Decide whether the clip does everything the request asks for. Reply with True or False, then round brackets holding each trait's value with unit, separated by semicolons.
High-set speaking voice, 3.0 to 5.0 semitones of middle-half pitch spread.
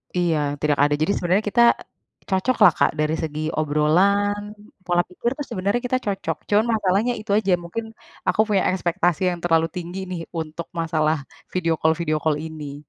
False (175 Hz; 4.2 semitones)